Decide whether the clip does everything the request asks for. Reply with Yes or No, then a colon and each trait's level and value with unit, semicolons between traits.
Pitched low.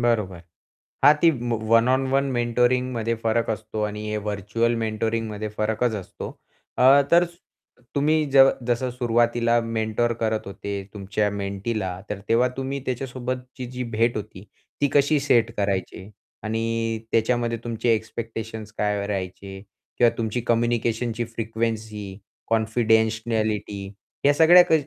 Yes: low, 115 Hz